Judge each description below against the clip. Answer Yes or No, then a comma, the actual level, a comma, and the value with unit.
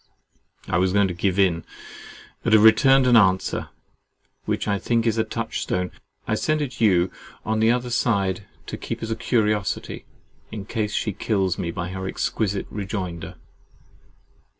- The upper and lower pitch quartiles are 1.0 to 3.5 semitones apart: Yes, average, 3.2 semitones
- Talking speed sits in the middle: Yes, average, 165 wpm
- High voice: No, low, 105 Hz